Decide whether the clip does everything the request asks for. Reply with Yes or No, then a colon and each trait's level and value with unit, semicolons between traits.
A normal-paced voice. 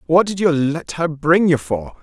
No: fast, 235 wpm